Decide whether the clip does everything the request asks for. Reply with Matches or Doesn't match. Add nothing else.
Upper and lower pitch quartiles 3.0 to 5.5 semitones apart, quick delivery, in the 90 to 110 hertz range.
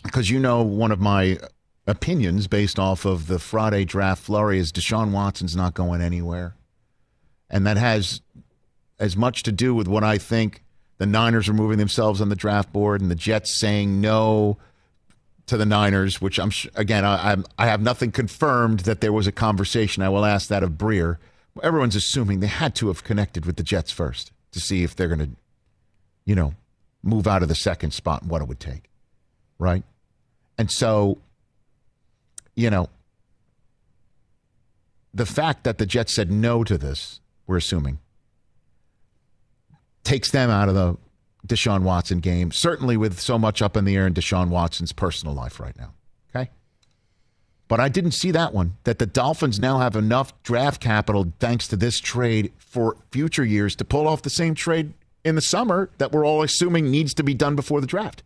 Doesn't match